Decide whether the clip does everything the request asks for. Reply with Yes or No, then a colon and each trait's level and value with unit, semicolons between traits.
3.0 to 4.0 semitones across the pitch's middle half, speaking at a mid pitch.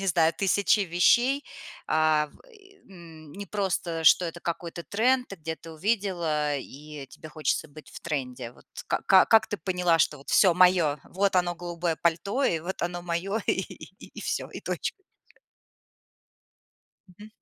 Yes: average, 3.7 semitones; medium, 175 Hz